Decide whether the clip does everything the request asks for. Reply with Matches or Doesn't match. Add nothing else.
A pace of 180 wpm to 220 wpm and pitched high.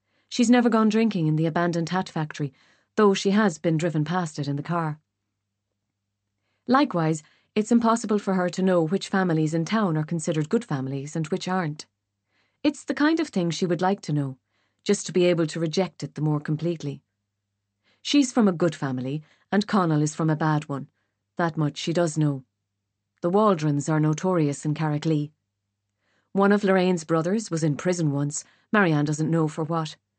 Doesn't match